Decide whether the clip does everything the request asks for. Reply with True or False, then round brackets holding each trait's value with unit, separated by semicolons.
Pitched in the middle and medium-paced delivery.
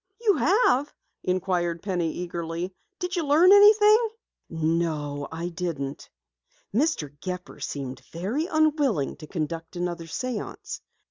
False (180 Hz; 115 wpm)